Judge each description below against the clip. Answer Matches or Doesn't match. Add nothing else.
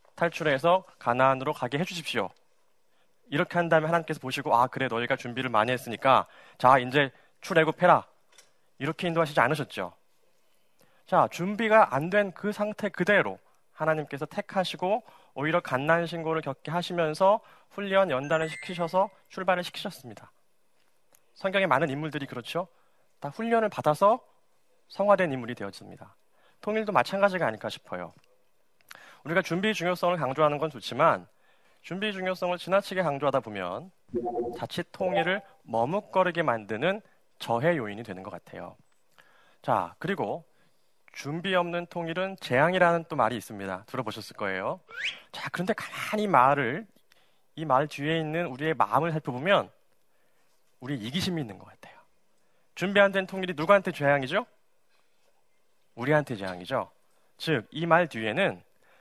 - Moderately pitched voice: Matches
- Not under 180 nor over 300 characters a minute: Doesn't match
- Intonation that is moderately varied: Doesn't match